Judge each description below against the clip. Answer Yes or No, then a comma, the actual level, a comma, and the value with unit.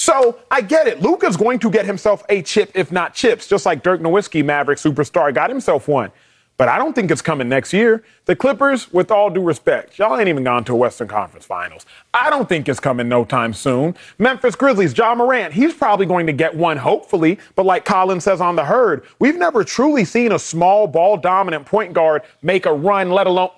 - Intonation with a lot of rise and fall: Yes, wide, 5.8 semitones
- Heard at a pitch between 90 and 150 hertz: No, high, 190 Hz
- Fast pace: Yes, fast, 220 wpm